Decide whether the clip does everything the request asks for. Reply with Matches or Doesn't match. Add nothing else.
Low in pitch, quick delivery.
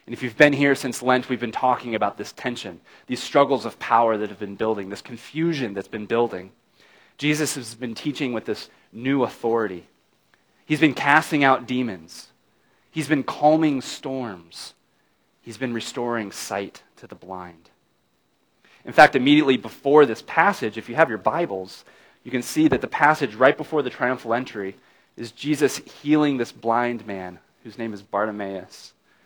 Doesn't match